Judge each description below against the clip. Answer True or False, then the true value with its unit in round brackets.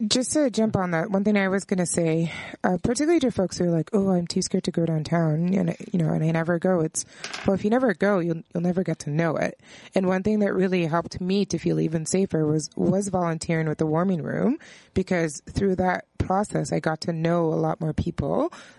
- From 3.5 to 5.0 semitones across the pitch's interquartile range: False (3.0 semitones)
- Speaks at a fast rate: True (245 wpm)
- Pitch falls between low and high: True (180 Hz)